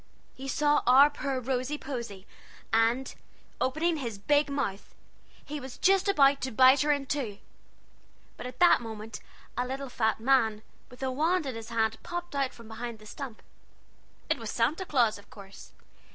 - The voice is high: Yes, very high, 260 Hz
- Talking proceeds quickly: No, average, 170 wpm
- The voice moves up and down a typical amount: Yes, average, 4.0 semitones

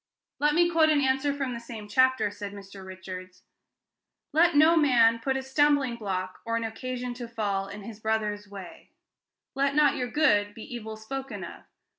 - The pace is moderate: Yes, average, 180 wpm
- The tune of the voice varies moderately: Yes, average, 4.8 semitones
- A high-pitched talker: Yes, high, 235 Hz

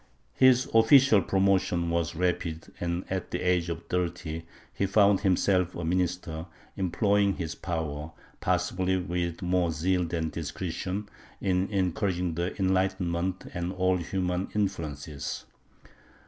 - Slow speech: Yes, slow, 120 wpm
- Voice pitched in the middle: No, very low, 90 Hz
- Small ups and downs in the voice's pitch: Yes, narrow, 2.0 semitones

